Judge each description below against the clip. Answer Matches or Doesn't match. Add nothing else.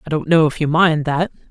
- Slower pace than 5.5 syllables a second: Doesn't match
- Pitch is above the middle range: Doesn't match